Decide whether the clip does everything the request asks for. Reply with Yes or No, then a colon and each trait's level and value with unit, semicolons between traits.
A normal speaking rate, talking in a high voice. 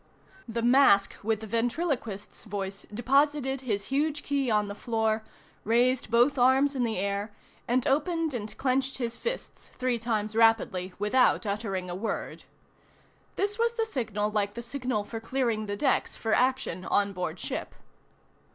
Yes: average, 155 wpm; high, 235 Hz